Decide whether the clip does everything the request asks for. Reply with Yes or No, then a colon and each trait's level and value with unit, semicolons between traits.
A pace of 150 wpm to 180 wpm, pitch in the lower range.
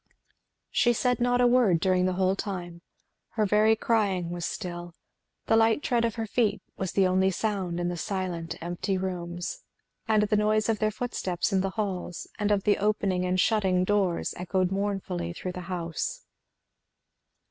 No: average, 175 wpm; high, 190 Hz